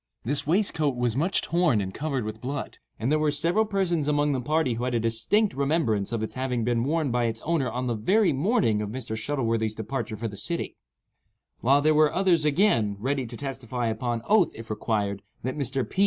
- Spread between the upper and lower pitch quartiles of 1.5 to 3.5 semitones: No, average, 5.2 semitones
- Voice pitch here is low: Yes, low, 130 Hz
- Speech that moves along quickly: Yes, fast, 210 wpm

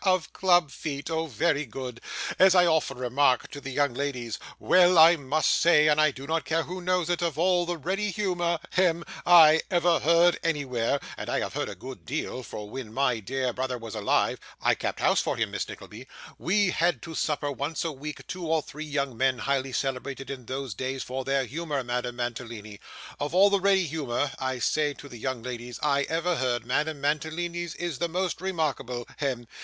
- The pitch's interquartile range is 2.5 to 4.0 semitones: No, average, 4.7 semitones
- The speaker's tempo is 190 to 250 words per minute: Yes, average, 200 wpm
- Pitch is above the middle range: No, medium, 145 Hz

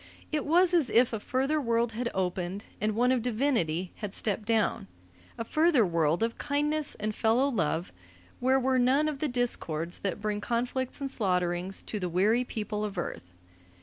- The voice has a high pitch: Yes, high, 230 Hz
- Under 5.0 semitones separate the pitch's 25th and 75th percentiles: No, average, 5.3 semitones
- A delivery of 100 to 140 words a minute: No, average, 175 wpm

